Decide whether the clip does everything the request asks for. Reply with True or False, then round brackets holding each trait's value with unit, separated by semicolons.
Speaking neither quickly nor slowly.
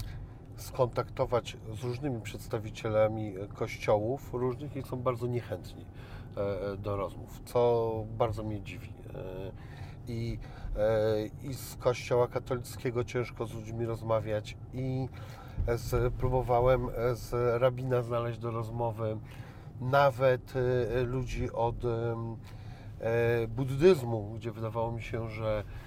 False (95 wpm)